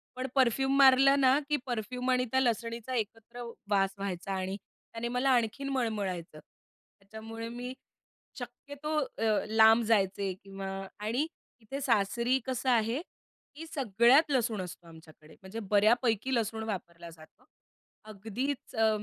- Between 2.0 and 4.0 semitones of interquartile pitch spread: No, average, 4.5 semitones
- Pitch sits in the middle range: No, high, 225 Hz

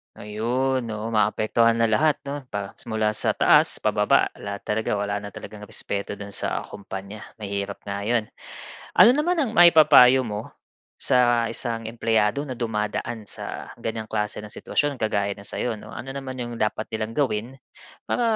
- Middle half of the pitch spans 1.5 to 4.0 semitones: Yes, average, 3.3 semitones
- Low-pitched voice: Yes, low, 110 Hz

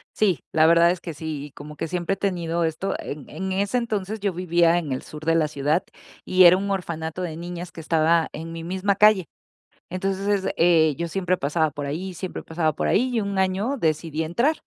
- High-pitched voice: No, medium, 170 Hz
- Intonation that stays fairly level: No, average, 3.1 semitones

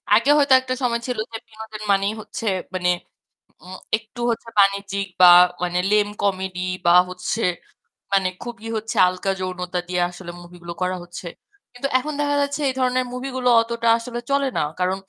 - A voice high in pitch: Yes, high, 210 Hz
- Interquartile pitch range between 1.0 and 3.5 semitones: No, average, 4.8 semitones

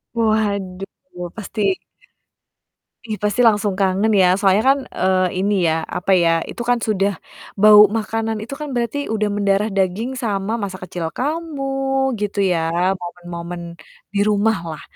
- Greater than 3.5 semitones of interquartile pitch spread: No, average, 3.2 semitones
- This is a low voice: No, high, 200 Hz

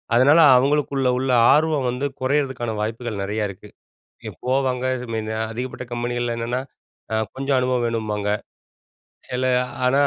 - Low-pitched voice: Yes, low, 125 Hz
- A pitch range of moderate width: No, narrow, 2.3 semitones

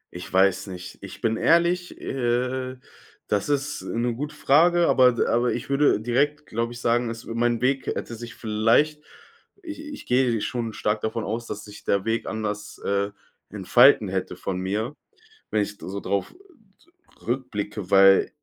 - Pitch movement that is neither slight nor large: Yes, average, 4.0 semitones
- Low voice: Yes, low, 115 Hz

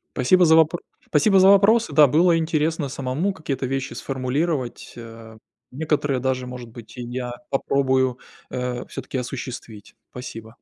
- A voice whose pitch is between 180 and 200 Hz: No, low, 130 Hz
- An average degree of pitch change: Yes, average, 4.2 semitones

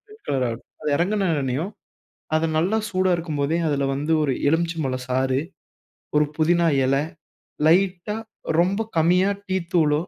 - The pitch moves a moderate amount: Yes, average, 4.4 semitones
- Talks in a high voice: No, medium, 160 Hz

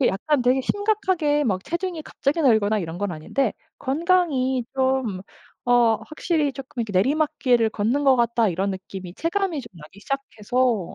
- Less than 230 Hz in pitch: No, very high, 255 Hz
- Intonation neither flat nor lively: No, wide, 6.0 semitones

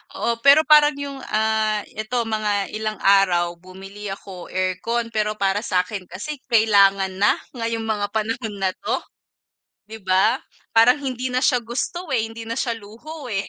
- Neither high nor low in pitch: No, high, 215 Hz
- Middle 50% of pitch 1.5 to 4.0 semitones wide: Yes, average, 3.3 semitones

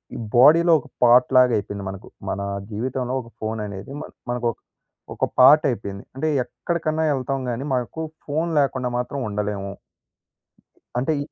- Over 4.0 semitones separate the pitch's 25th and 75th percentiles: Yes, average, 4.6 semitones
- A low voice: Yes, low, 125 Hz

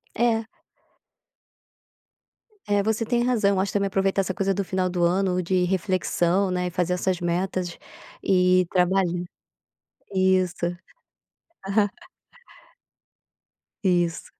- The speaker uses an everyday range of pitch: No, narrow, 1.6 semitones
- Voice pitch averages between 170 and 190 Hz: Yes, medium, 185 Hz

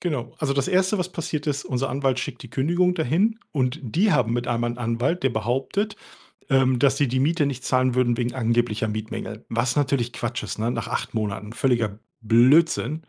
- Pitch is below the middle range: Yes, low, 130 Hz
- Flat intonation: No, average, 4.1 semitones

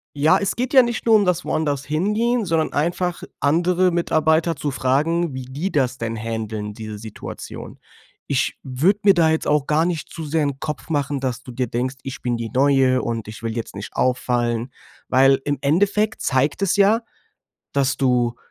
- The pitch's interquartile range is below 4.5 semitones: No, average, 5.2 semitones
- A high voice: No, medium, 145 Hz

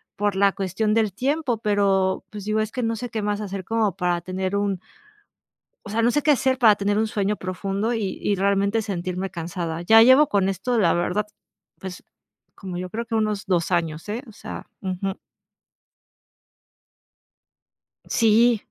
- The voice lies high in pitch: Yes, high, 205 Hz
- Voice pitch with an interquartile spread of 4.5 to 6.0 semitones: No, average, 2.9 semitones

